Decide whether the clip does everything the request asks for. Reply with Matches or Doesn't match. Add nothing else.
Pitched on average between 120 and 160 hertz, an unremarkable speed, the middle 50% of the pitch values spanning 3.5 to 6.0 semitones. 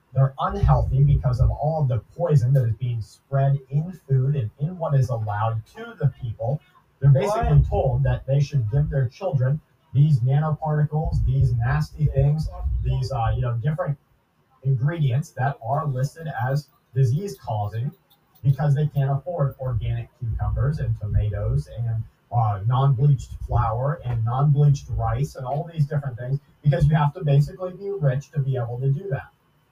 Doesn't match